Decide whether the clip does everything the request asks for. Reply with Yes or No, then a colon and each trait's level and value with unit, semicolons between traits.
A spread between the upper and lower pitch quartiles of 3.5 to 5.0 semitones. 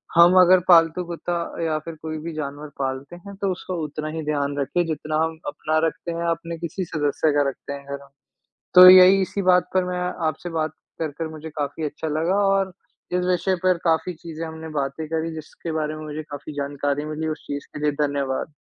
No: average, 2.7 semitones